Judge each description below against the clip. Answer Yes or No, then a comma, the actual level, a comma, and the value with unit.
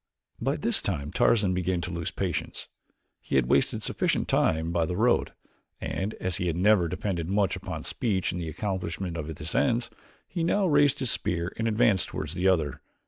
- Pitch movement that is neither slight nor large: Yes, average, 4.4 semitones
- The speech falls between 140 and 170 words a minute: No, average, 190 wpm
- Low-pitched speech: Yes, very low, 90 Hz